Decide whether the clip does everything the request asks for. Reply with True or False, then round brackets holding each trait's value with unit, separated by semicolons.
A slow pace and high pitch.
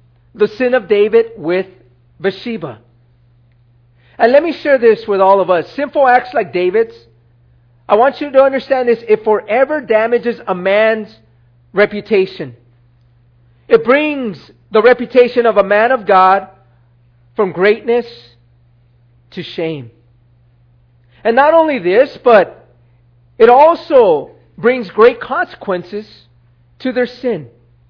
True (125 wpm; 195 Hz)